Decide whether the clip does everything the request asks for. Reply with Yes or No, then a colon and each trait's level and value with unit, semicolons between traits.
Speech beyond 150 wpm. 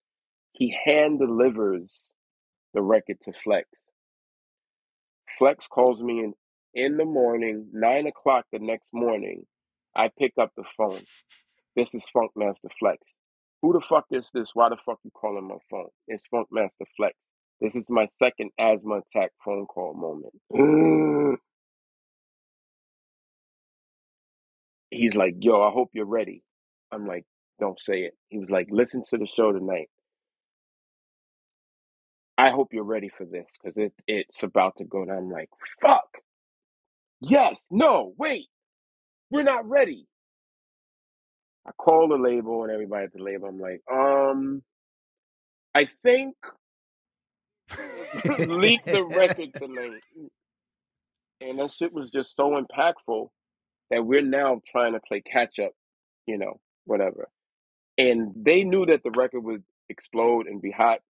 No: average, 140 wpm